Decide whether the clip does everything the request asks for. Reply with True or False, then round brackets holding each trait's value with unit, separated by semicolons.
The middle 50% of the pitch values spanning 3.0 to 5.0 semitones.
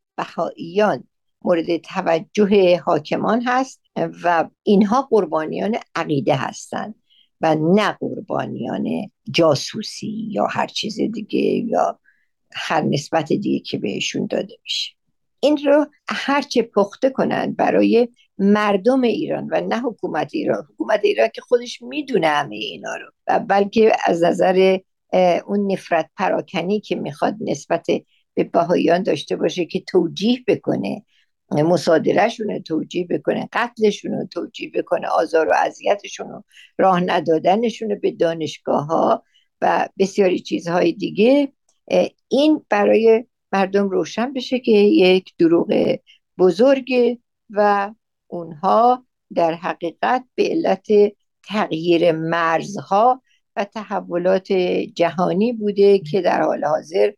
False (5.4 semitones)